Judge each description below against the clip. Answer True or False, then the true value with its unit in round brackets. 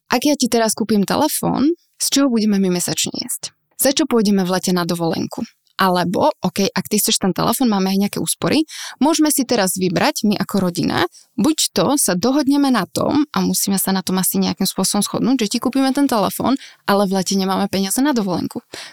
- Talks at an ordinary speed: False (205 wpm)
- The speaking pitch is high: True (210 Hz)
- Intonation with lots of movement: True (5.8 semitones)